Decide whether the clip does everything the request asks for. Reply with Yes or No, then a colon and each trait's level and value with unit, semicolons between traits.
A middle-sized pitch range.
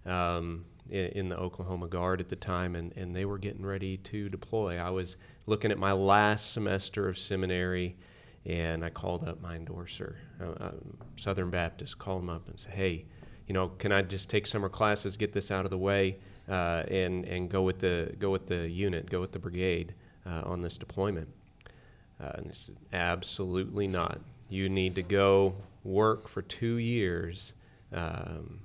No: narrow, 2.1 semitones